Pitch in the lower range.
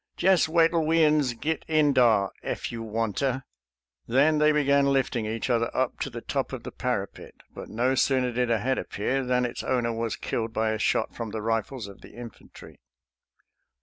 Yes: low, 125 Hz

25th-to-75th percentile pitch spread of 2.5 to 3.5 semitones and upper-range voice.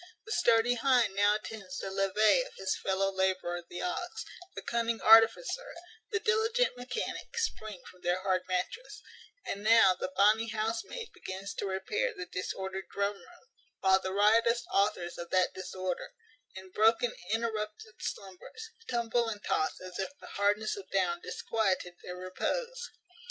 No: average, 3.9 semitones; high, 210 Hz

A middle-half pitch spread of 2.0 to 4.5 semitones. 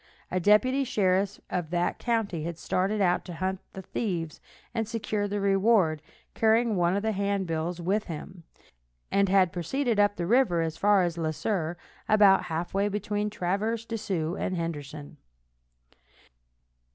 Yes: average, 3.5 semitones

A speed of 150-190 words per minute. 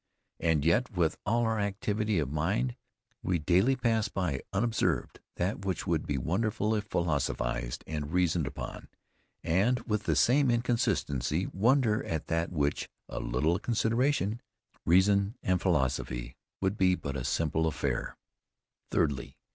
No: average, 140 wpm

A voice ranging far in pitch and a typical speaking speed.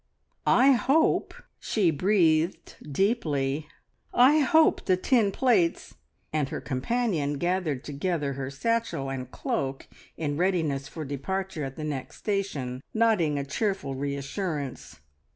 No: wide, 6.5 semitones; slow, 130 wpm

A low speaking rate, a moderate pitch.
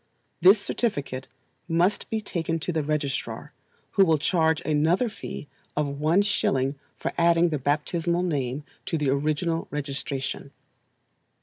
Yes: slow, 130 wpm; medium, 155 Hz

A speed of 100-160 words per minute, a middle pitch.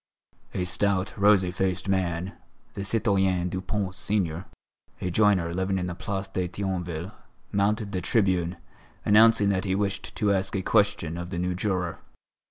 No: average, 155 wpm; very low, 95 Hz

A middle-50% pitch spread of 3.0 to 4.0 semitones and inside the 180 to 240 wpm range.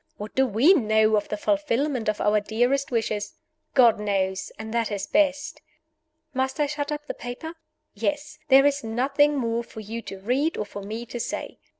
No: average, 4.9 semitones; average, 190 wpm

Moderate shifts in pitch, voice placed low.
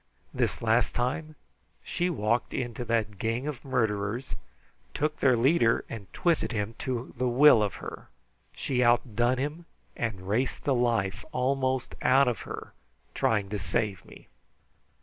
Yes: average, 3.0 semitones; low, 120 Hz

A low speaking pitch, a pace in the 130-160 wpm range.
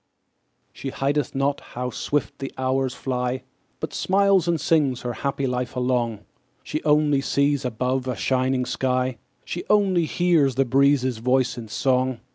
Yes: low, 130 Hz; average, 150 wpm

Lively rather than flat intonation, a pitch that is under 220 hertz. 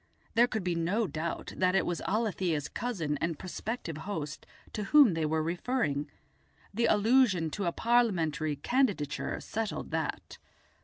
Yes: wide, 6.0 semitones; medium, 185 Hz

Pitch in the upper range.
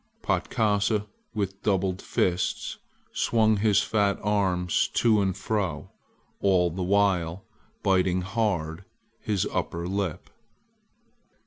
No: very low, 95 Hz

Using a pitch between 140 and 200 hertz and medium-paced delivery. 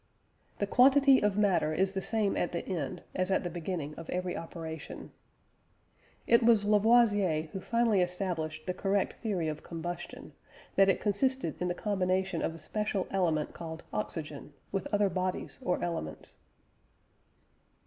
Yes: medium, 185 Hz; average, 150 wpm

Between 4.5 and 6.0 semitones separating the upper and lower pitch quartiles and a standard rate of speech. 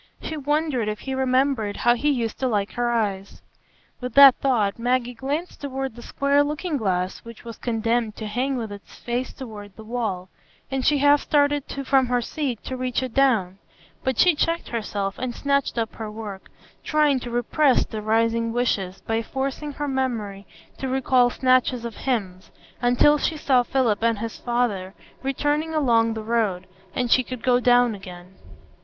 No: average, 3.5 semitones; average, 175 wpm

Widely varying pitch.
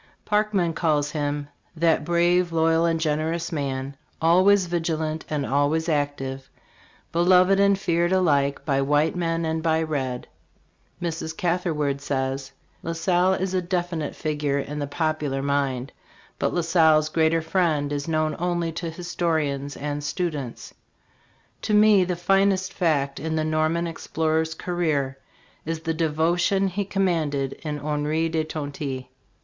No: average, 2.9 semitones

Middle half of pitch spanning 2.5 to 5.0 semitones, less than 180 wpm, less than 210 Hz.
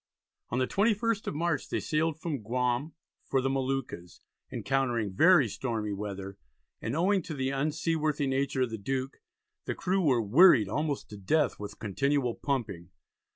No: wide, 5.4 semitones; average, 155 wpm; low, 135 Hz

